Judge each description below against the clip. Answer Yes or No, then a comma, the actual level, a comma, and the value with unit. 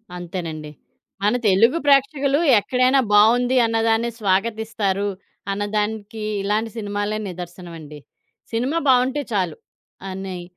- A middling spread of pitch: Yes, average, 3.9 semitones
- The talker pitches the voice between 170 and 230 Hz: Yes, high, 210 Hz